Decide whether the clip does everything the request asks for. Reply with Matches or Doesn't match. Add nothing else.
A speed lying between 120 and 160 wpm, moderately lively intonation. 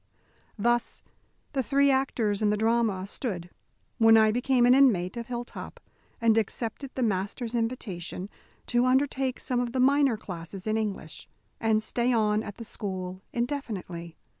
Matches